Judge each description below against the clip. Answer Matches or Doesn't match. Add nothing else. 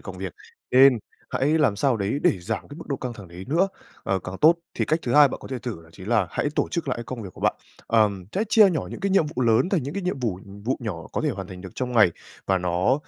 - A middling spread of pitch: Doesn't match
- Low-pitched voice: Matches